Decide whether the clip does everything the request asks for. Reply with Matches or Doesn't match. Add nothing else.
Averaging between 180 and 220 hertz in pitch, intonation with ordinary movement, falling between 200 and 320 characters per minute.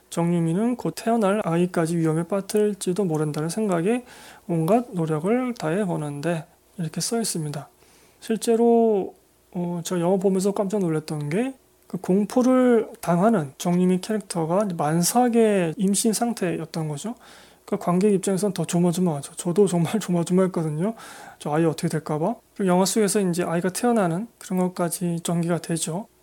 Doesn't match